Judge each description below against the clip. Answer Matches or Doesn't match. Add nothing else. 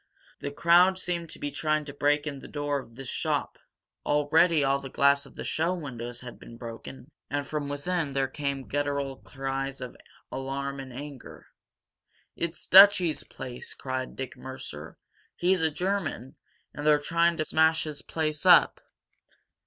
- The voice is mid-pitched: Matches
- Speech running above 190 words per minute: Doesn't match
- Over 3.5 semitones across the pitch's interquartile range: Doesn't match